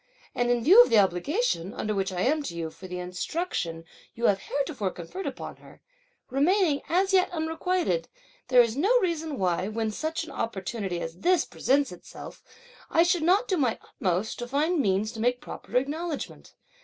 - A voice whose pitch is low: No, very high, 255 Hz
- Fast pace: No, average, 180 wpm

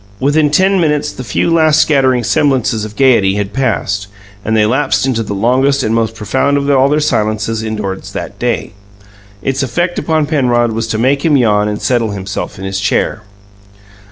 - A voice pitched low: Yes, low, 125 Hz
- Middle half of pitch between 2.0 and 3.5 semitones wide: No, average, 4.8 semitones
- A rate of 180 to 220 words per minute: Yes, average, 185 wpm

